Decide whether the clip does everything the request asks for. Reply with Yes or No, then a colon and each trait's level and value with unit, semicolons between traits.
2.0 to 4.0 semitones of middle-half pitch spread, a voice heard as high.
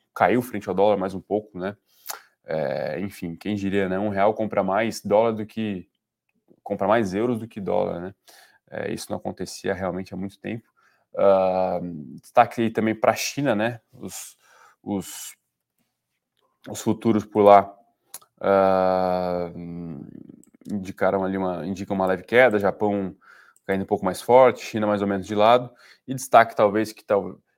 No: narrow, 2.6 semitones; low, 100 Hz